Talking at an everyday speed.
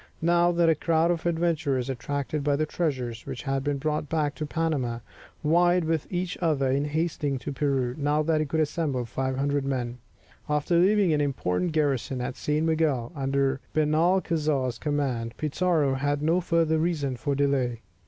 Yes: average, 165 wpm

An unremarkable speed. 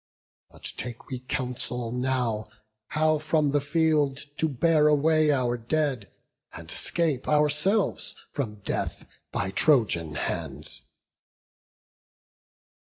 No: slow, 105 wpm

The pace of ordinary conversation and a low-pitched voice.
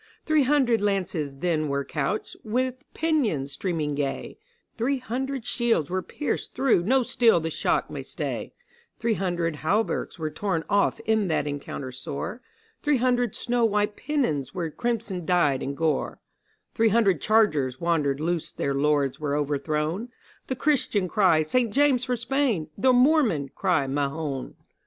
No: average, 150 wpm; high, 190 Hz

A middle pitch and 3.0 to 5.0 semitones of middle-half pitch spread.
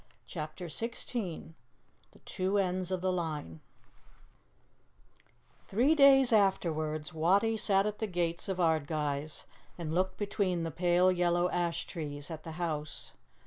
Yes: medium, 175 Hz; average, 3.5 semitones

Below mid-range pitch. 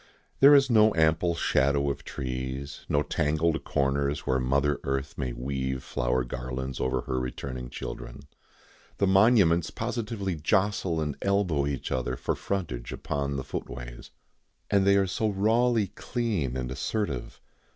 Yes: very low, 70 Hz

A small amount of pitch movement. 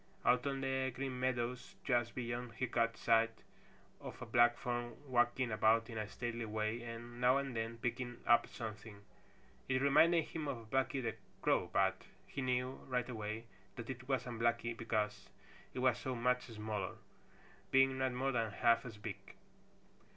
Yes: narrow, 2.0 semitones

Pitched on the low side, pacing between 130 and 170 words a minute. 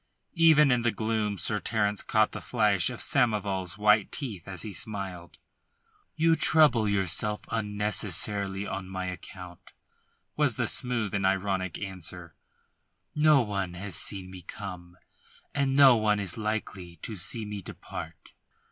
Yes: low, 105 Hz; average, 140 wpm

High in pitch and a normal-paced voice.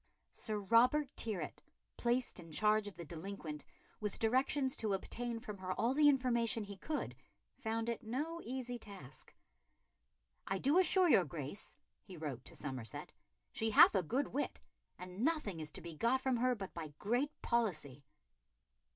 Yes: high, 220 Hz; average, 160 wpm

